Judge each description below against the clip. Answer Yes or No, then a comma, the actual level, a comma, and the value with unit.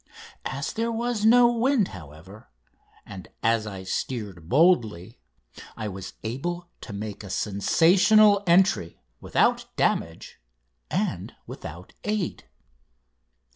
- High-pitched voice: No, low, 115 Hz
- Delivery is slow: Yes, slow, 105 wpm